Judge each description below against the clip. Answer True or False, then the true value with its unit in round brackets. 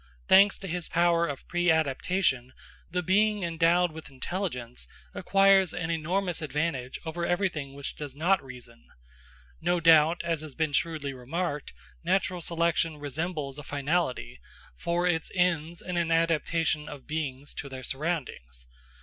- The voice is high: False (165 Hz)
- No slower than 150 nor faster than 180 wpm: False (140 wpm)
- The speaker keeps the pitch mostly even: False (3.6 semitones)